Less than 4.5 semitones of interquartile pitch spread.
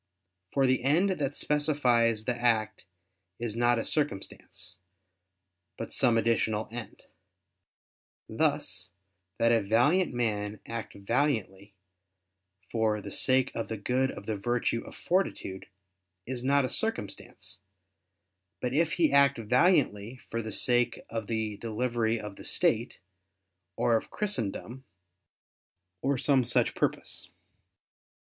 Yes: average, 3.7 semitones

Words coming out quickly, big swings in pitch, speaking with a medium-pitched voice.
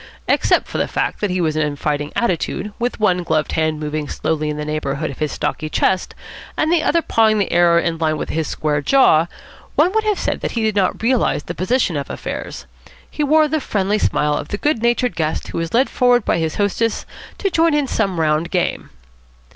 Yes: fast, 220 wpm; wide, 7.5 semitones; medium, 180 Hz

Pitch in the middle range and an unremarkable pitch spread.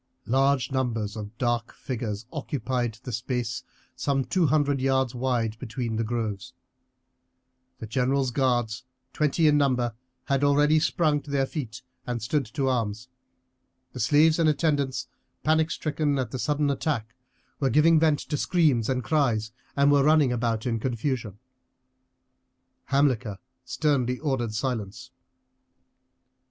No: low, 130 Hz; average, 3.6 semitones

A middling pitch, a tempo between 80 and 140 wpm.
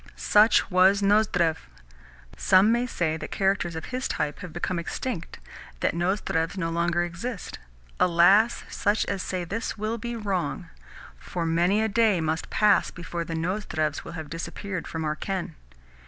No: medium, 180 Hz; average, 155 wpm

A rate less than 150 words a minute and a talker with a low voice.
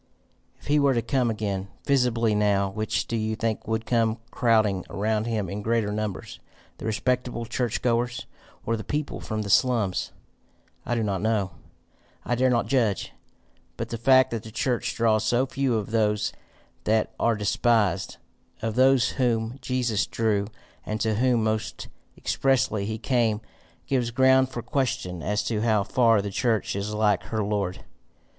No: average, 165 wpm; low, 110 Hz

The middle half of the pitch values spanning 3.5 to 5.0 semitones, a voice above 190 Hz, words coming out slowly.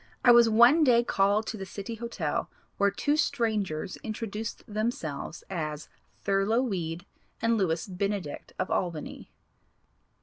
Yes: average, 4.2 semitones; high, 205 Hz; slow, 130 wpm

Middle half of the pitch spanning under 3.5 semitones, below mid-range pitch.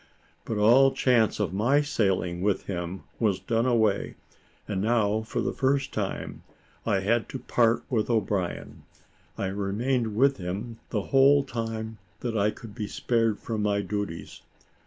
Yes: average, 3.0 semitones; low, 110 Hz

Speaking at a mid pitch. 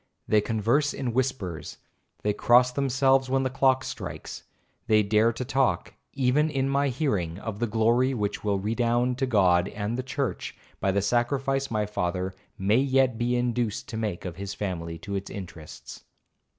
No: low, 115 Hz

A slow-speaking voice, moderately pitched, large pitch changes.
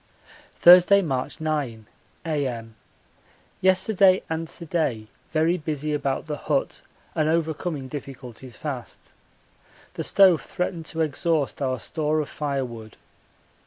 No: slow, 115 wpm; medium, 150 Hz; average, 3.8 semitones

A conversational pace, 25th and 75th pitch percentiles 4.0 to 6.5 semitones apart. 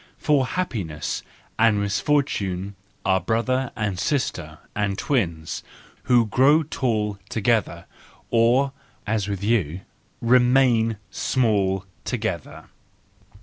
No: slow, 95 wpm; average, 4.5 semitones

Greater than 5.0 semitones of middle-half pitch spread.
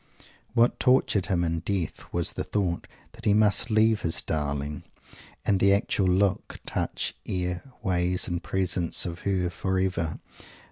No: narrow, 2.6 semitones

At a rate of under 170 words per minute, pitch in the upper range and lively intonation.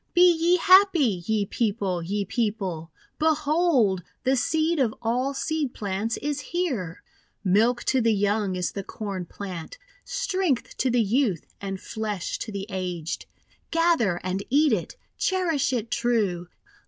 Yes: average, 145 wpm; high, 225 Hz; wide, 7.3 semitones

